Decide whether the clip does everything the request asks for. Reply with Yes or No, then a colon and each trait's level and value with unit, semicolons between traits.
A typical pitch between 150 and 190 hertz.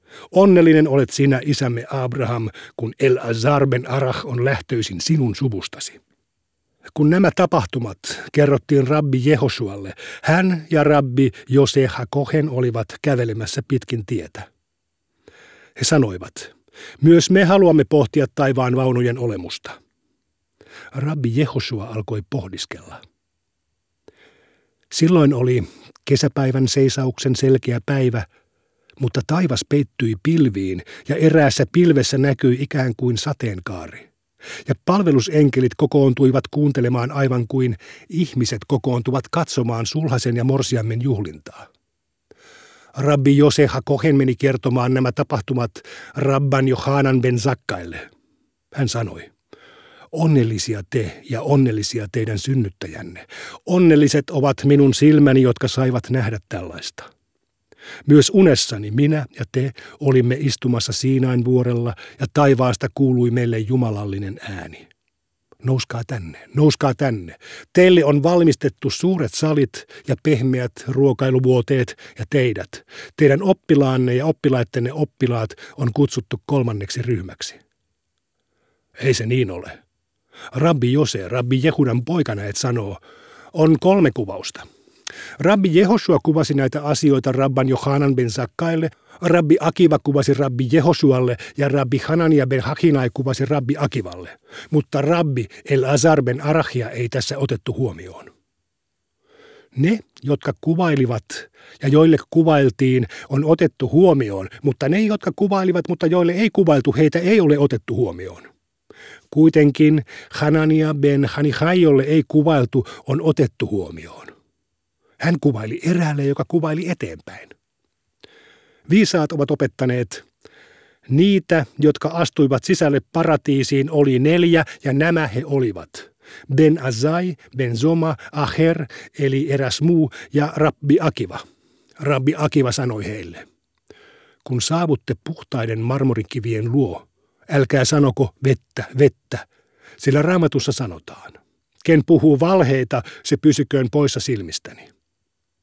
No: low, 135 Hz